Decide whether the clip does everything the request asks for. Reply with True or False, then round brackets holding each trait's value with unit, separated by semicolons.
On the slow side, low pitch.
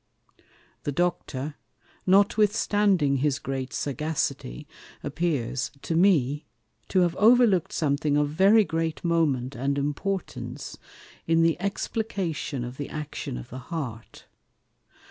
False (110 wpm; 155 Hz)